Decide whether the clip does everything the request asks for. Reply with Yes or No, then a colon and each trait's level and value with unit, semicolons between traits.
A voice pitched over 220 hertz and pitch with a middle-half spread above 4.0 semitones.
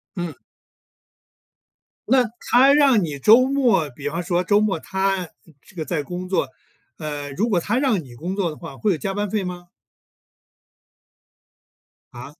No: medium, 185 Hz; average, 4.7 semitones